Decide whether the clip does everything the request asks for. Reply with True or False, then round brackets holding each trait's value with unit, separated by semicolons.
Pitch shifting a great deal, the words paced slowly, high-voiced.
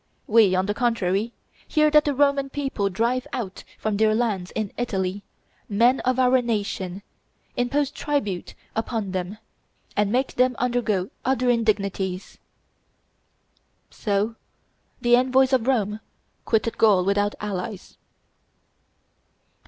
False (4.0 semitones; 120 wpm; 225 Hz)